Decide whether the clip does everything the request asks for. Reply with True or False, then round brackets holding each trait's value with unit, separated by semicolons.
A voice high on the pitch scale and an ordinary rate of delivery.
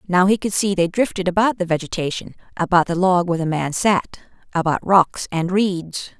False (180 Hz; 195 wpm)